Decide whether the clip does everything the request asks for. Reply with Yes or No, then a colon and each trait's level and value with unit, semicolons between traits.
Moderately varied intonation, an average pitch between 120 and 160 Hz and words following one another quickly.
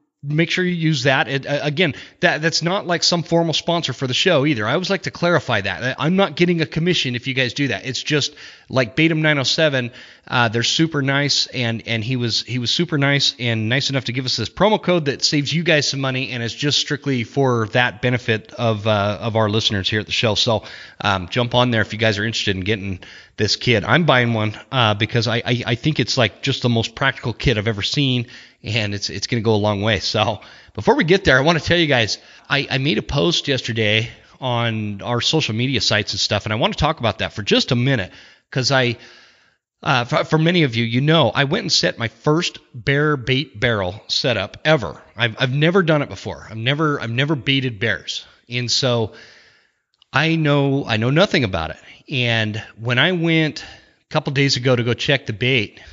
Yes: average, 4.7 semitones; low, 125 Hz; fast, 230 wpm